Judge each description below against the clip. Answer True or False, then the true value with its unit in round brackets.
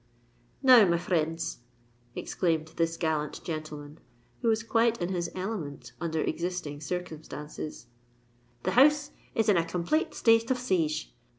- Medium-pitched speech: True (170 Hz)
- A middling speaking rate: False (130 wpm)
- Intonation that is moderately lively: False (6.0 semitones)